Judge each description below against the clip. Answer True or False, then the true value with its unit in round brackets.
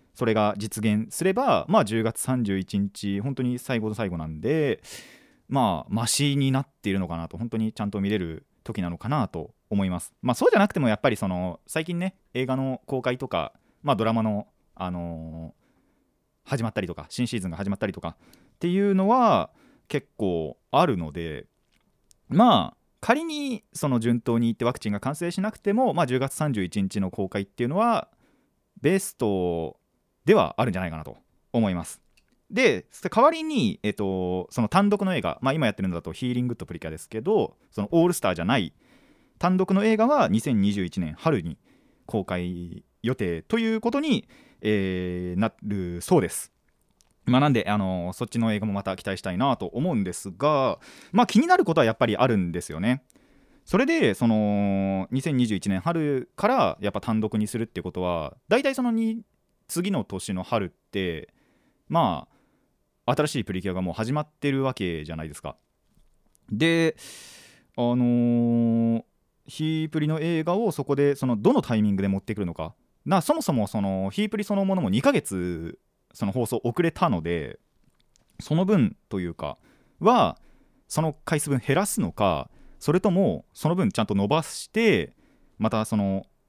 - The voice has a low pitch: True (115 Hz)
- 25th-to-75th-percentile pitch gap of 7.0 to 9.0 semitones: True (8.6 semitones)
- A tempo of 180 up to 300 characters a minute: False (325 characters per minute)